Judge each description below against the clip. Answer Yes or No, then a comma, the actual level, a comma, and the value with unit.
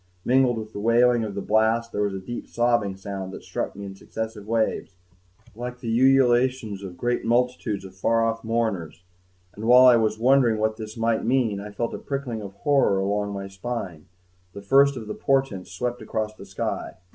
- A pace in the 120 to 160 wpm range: No, average, 195 wpm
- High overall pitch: No, low, 110 Hz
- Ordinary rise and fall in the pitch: Yes, average, 3.3 semitones